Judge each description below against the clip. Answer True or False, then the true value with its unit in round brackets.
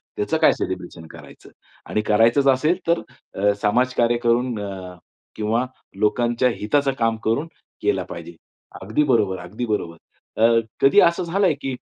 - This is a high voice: False (115 Hz)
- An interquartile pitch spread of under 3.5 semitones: False (4.5 semitones)